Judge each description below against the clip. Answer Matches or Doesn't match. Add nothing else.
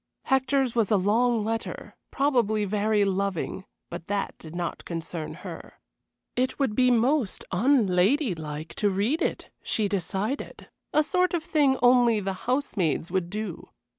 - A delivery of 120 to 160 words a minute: Matches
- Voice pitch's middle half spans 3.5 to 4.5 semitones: Doesn't match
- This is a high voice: Matches